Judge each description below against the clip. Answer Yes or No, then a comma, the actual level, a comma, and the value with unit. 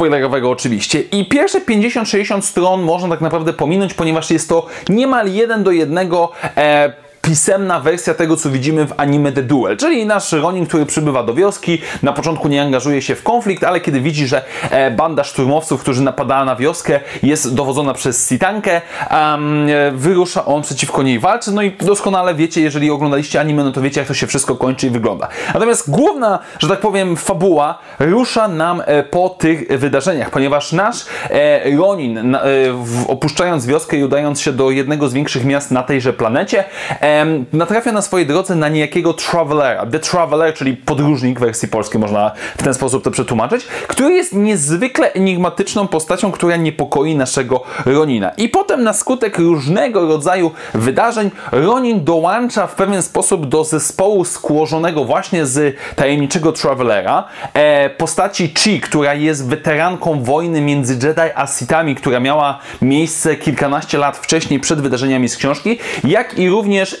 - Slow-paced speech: No, fast, 160 wpm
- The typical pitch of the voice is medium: Yes, medium, 155 Hz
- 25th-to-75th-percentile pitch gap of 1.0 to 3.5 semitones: No, average, 4.5 semitones